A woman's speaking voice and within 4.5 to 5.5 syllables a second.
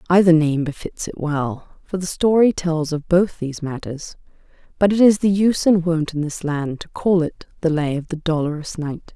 Yes: female; 5.0 syllables/s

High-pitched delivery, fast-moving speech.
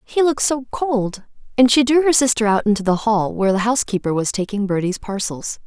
Yes: high, 220 Hz; fast, 210 wpm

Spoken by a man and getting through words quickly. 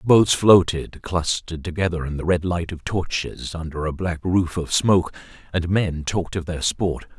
No: male; average, 190 wpm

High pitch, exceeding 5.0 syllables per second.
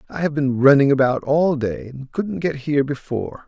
No: medium, 140 Hz; 5.2 syllables/s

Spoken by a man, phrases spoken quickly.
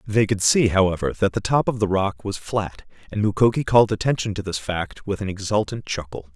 Yes: male; fast, 215 wpm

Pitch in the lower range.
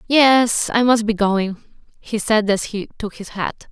No: high, 215 Hz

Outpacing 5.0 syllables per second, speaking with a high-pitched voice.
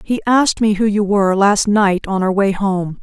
No: 4.9 syllables/s; high, 200 Hz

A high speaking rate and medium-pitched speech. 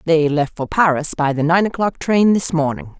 Yes: fast, 220 wpm; medium, 160 Hz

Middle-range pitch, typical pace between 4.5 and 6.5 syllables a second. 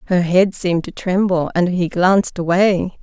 Yes: medium, 180 Hz; 4.7 syllables/s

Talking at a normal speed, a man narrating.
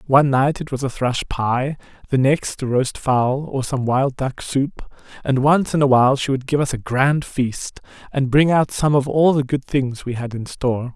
No: fast, 230 wpm; male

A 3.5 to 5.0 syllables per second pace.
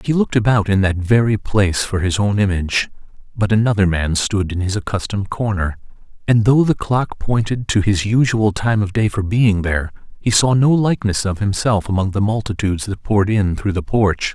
No: 5.4 syllables/s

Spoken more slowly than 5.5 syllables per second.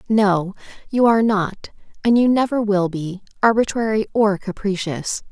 Yes: 4.6 syllables/s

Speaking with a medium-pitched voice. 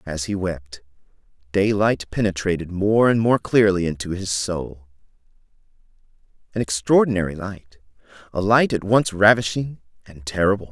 No: very low, 95 Hz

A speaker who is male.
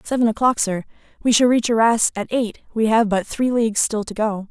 No: female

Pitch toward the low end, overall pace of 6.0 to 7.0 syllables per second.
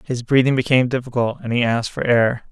Yes: low, 125 Hz; 6.4 syllables/s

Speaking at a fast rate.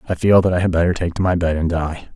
Yes: fast, 335 wpm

